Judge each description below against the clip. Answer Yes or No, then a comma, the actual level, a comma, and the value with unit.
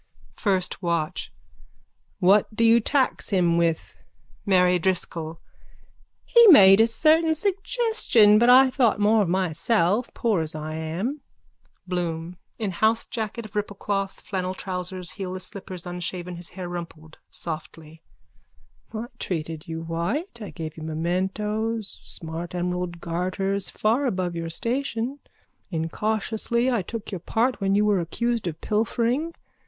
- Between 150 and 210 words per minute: No, slow, 135 wpm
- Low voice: No, high, 190 Hz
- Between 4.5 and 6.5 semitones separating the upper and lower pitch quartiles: Yes, average, 4.8 semitones